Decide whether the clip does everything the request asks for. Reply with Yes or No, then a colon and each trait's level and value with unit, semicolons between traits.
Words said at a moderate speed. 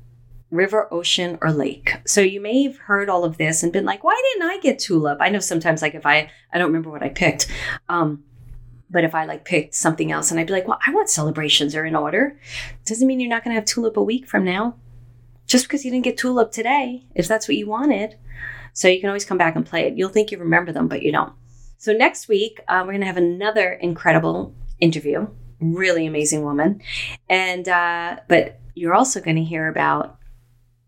No: fast, 225 wpm